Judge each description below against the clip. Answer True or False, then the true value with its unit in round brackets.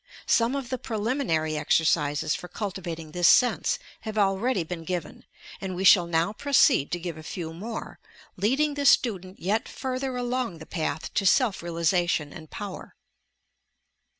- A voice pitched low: False (190 Hz)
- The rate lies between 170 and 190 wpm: False (155 wpm)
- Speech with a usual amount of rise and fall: False (6.1 semitones)